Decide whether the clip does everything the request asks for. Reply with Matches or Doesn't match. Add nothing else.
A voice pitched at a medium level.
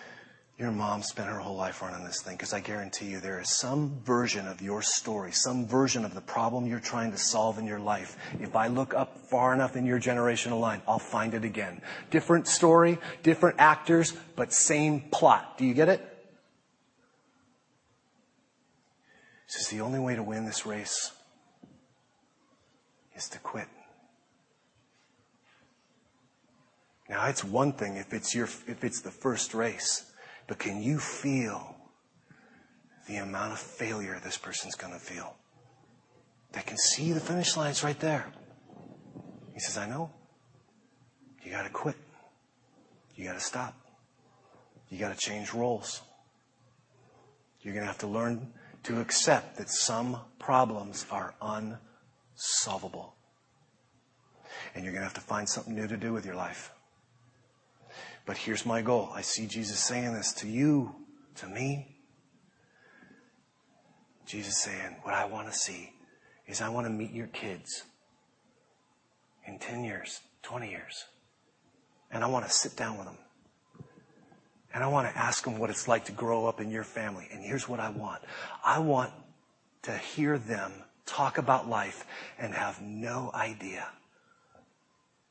Doesn't match